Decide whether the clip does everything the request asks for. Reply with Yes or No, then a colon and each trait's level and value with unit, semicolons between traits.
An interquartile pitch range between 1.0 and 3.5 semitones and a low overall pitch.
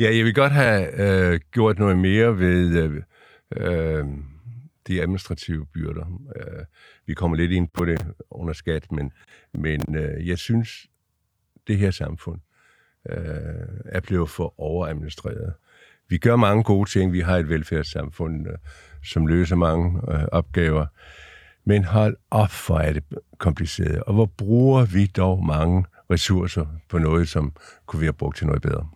No: average, 4.0 semitones; very low, 90 Hz